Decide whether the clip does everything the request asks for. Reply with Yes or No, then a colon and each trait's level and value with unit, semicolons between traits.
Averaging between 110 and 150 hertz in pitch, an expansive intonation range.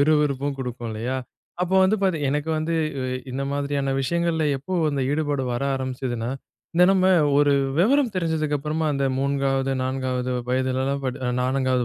No: medium, 140 Hz; average, 3.2 semitones